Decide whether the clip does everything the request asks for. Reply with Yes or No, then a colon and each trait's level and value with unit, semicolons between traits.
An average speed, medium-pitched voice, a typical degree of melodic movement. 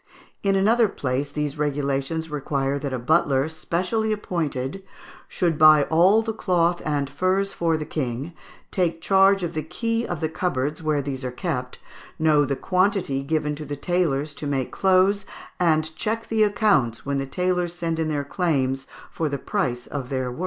Yes: average, 175 wpm; medium, 155 Hz; average, 4.6 semitones